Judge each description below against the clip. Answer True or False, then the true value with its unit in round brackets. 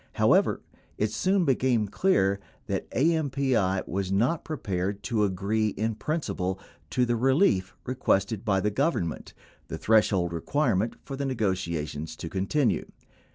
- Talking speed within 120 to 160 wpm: True (140 wpm)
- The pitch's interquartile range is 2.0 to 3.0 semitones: False (5.6 semitones)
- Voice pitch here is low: True (110 Hz)